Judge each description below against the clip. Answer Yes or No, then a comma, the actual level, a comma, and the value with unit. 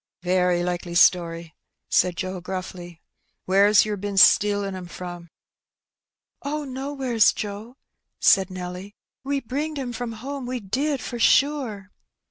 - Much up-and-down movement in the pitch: Yes, wide, 6.0 semitones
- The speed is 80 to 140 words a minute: Yes, slow, 135 wpm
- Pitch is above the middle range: Yes, high, 205 Hz